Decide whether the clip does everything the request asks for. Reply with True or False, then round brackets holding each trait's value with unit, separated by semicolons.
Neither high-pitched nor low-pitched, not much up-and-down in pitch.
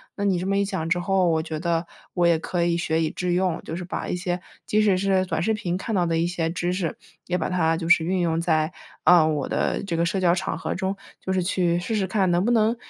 True (175 Hz; 2.1 semitones)